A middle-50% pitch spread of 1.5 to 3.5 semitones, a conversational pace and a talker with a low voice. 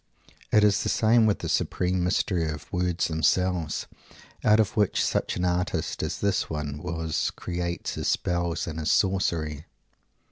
Yes: average, 2.9 semitones; average, 155 wpm; very low, 90 Hz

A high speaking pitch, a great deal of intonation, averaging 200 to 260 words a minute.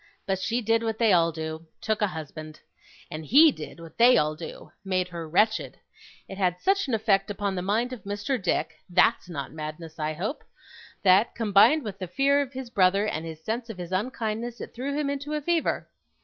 Yes: high, 200 Hz; wide, 6.0 semitones; fast, 205 wpm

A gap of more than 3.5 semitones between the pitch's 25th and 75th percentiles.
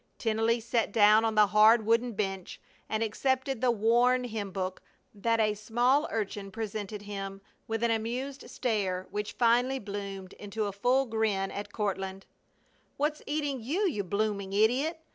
No: average, 3.2 semitones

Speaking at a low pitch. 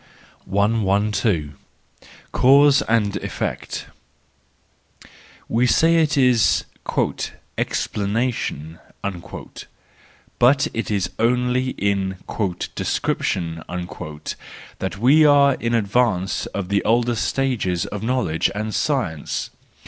Yes: low, 110 Hz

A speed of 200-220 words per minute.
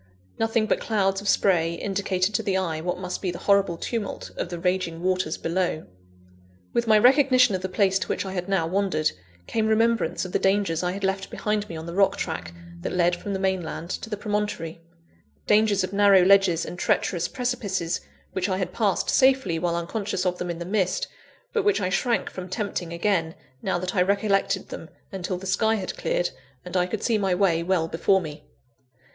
Yes: fast, 205 wpm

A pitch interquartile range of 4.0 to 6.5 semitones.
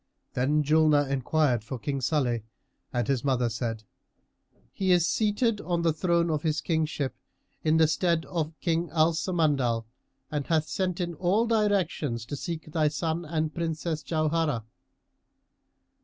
No: average, 3.3 semitones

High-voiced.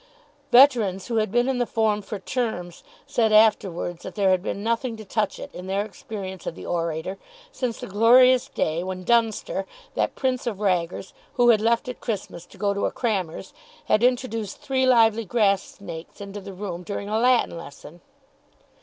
Yes: high, 210 Hz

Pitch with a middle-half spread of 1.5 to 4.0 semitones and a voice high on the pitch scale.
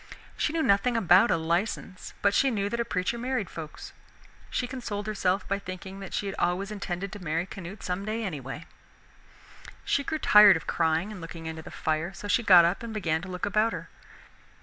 Yes: average, 3.6 semitones; high, 195 Hz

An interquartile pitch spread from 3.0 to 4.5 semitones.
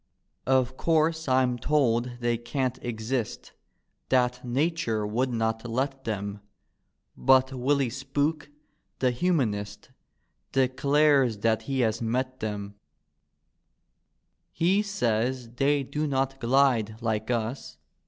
Yes: average, 3.3 semitones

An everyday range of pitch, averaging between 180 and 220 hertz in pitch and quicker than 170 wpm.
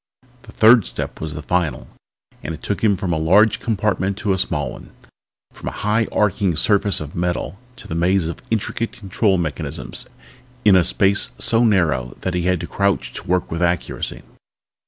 No: average, 3.7 semitones; very low, 95 Hz; average, 190 wpm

